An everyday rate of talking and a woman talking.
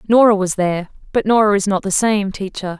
Yes: average, 195 wpm; female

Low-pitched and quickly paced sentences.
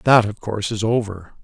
Yes: low, 105 Hz; fast, 210 wpm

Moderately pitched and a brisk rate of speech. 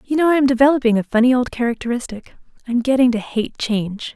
No: high, 245 Hz; fast, 215 wpm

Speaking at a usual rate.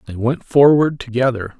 Yes: average, 150 wpm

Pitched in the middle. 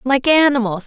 No: very high, 255 Hz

